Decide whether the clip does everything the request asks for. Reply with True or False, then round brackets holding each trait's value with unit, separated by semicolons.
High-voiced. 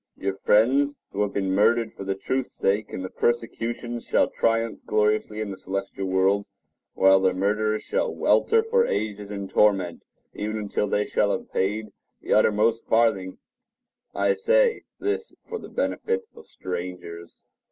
False (105 Hz)